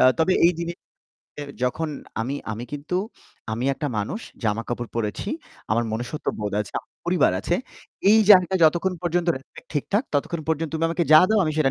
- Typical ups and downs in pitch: No, wide, 6.3 semitones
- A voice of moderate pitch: Yes, medium, 155 Hz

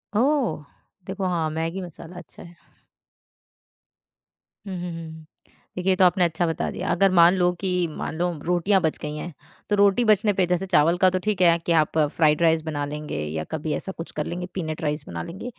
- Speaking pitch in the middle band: Yes, medium, 175 Hz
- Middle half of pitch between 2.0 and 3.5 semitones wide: Yes, average, 2.9 semitones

